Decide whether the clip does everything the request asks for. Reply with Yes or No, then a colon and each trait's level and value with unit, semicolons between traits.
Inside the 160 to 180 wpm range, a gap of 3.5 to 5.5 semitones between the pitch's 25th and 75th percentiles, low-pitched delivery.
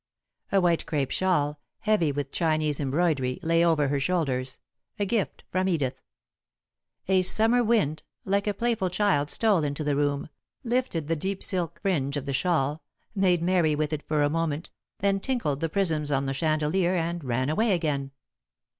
No: average, 170 wpm; average, 4.5 semitones; medium, 165 Hz